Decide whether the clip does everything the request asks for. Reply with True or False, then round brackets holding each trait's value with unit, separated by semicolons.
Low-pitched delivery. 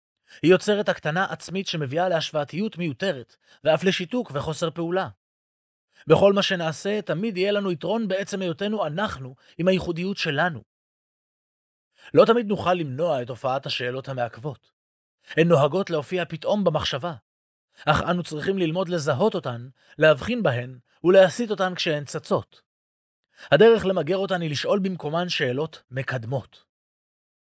False (170 Hz)